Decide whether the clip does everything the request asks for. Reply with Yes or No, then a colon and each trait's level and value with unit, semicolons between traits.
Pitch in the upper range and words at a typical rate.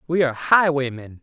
No: medium, 145 Hz; average, 145 wpm